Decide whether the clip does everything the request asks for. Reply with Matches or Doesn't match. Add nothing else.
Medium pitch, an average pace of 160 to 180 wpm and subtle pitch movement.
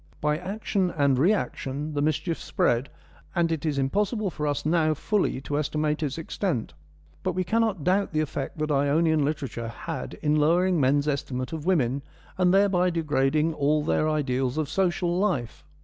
Doesn't match